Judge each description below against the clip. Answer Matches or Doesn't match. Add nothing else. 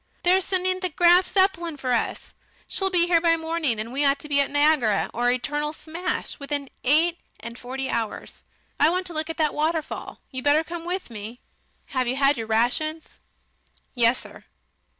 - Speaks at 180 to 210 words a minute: Matches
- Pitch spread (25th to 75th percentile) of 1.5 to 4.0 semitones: Doesn't match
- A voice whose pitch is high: Matches